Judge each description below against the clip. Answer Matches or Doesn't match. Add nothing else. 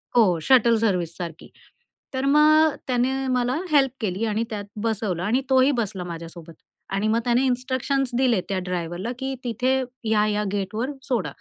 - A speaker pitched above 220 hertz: Matches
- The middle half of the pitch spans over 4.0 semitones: Matches